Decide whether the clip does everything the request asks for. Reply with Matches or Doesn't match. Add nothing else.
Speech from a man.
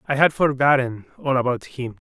Matches